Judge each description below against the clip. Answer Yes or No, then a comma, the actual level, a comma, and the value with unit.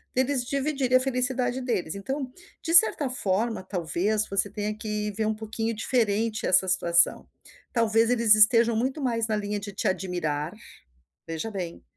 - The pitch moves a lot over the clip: No, average, 3.9 semitones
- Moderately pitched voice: No, high, 220 Hz